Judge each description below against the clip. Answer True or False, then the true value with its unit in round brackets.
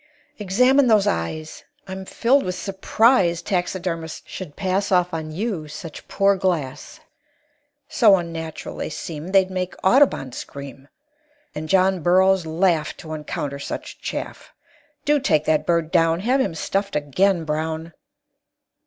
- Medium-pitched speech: True (180 Hz)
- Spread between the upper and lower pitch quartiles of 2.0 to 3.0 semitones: False (3.7 semitones)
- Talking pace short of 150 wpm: True (135 wpm)